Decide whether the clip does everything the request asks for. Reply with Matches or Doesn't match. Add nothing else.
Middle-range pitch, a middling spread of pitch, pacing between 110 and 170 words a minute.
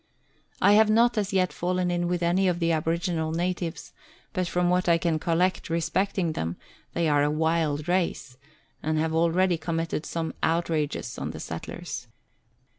Doesn't match